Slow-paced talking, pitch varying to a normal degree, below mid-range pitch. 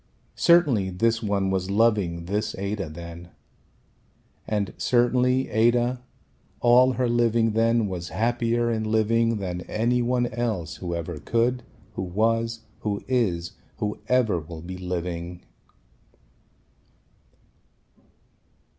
Yes: slow, 110 wpm; average, 4.6 semitones; low, 110 Hz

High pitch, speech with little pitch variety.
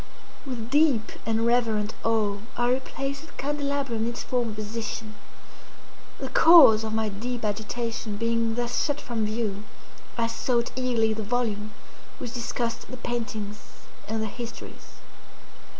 Yes: high, 230 Hz; narrow, 2.2 semitones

